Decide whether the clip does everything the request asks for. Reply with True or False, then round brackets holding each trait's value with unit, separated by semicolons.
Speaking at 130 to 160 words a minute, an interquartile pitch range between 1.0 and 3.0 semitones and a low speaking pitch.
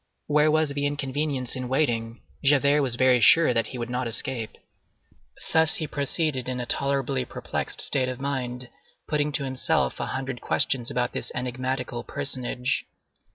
True (155 wpm; 2.4 semitones; 130 Hz)